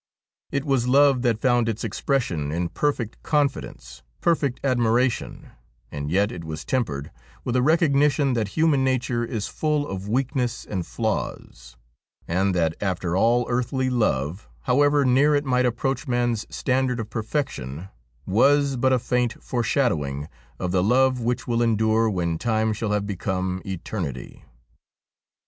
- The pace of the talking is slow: No, average, 145 wpm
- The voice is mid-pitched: No, low, 120 Hz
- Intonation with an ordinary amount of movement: No, wide, 5.7 semitones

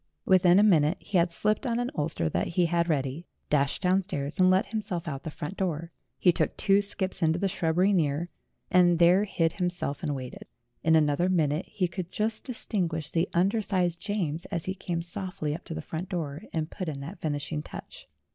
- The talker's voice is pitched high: No, medium, 175 Hz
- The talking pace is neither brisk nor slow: No, fast, 215 wpm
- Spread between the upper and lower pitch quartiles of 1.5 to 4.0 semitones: Yes, average, 3.3 semitones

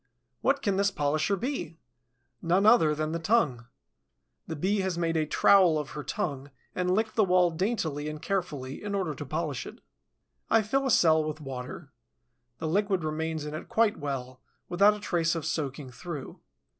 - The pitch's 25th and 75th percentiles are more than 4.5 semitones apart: Yes, average, 4.9 semitones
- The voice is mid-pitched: Yes, medium, 165 Hz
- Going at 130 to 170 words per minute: No, average, 180 wpm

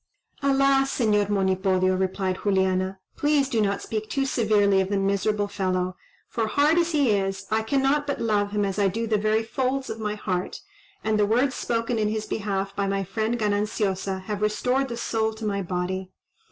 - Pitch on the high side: Yes, high, 210 Hz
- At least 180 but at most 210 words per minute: Yes, average, 190 wpm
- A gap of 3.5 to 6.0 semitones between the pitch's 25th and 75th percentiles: No, average, 3.0 semitones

